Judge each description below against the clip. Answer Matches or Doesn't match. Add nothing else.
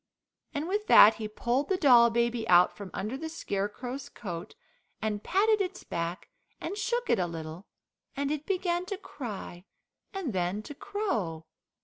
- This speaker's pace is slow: Doesn't match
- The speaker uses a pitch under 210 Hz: Doesn't match